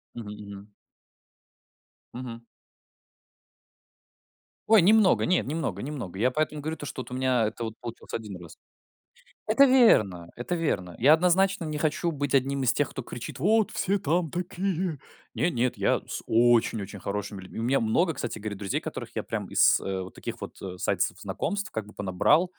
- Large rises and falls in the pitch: Yes, wide, 8.0 semitones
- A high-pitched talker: No, low, 130 Hz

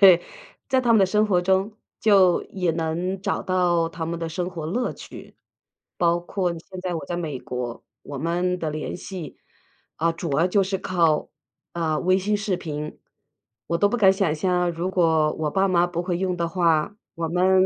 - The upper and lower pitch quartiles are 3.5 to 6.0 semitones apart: No, narrow, 2.4 semitones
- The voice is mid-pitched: Yes, medium, 175 Hz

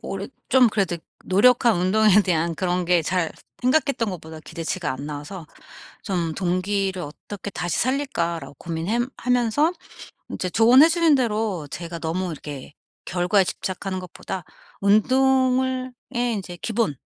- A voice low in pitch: No, high, 190 Hz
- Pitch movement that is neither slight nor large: No, wide, 5.8 semitones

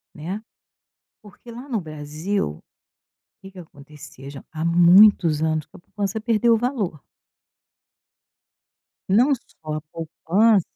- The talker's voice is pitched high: No, medium, 175 Hz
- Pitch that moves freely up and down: Yes, wide, 5.8 semitones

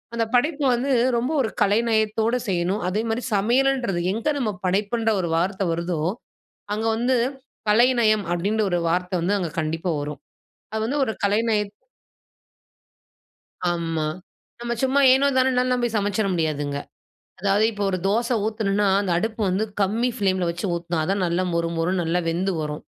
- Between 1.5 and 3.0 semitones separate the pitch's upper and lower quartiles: No, average, 4.8 semitones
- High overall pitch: Yes, high, 205 Hz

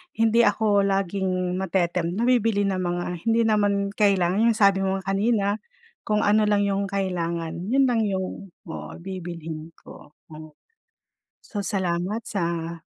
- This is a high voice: Yes, high, 195 Hz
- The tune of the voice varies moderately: Yes, average, 3.0 semitones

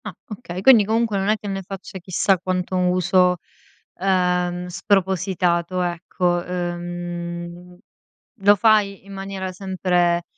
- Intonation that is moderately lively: No, narrow, 1.7 semitones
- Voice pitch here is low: No, medium, 185 Hz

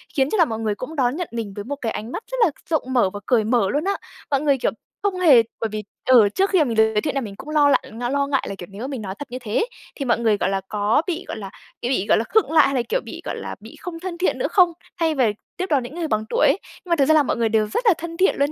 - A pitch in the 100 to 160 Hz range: No, very high, 270 Hz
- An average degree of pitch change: No, wide, 6.6 semitones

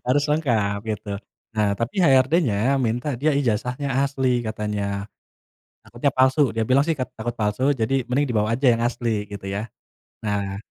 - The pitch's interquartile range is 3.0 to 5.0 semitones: Yes, average, 4.2 semitones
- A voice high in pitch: No, low, 120 Hz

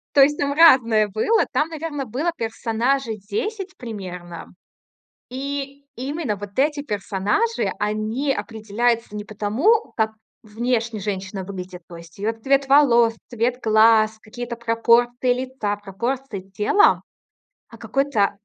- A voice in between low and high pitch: No, high, 230 Hz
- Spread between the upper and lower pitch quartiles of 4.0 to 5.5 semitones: Yes, average, 4.6 semitones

